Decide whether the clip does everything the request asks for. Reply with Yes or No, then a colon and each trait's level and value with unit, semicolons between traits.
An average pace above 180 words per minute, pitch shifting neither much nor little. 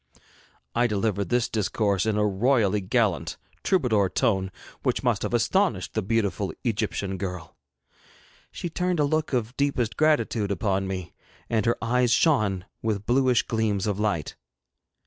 No: average, 145 wpm; average, 3.9 semitones